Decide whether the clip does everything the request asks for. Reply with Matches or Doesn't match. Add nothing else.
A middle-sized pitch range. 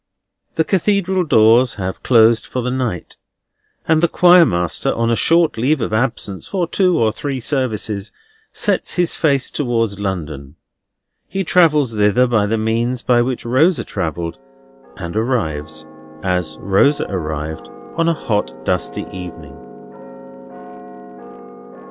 Doesn't match